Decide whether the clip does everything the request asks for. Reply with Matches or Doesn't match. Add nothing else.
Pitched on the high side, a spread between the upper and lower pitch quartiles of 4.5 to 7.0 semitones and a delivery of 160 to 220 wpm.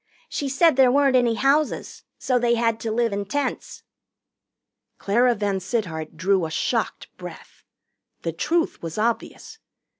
Doesn't match